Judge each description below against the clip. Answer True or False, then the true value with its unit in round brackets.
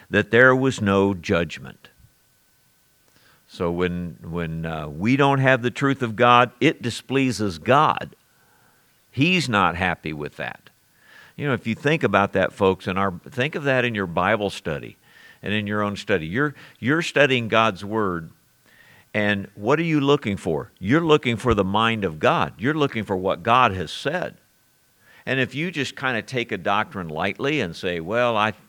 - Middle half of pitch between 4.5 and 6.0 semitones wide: True (5.2 semitones)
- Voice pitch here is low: True (110 Hz)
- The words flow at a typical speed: True (175 wpm)